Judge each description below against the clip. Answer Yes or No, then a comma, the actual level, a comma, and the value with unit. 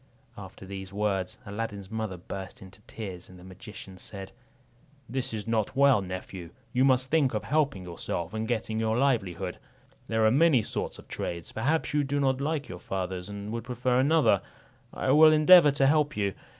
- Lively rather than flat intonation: Yes, wide, 5.9 semitones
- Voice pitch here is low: Yes, low, 110 Hz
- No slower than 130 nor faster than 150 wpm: No, average, 180 wpm